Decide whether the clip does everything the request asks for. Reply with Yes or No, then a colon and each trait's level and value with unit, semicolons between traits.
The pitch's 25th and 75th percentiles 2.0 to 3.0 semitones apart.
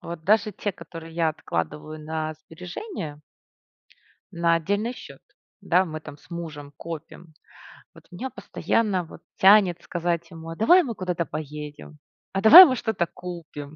No: average, 3.7 semitones